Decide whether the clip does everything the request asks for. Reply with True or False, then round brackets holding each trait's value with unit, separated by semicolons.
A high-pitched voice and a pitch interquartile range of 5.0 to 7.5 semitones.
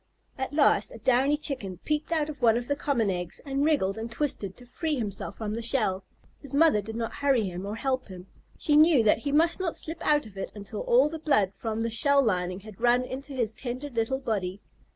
True (245 Hz; 5.3 semitones)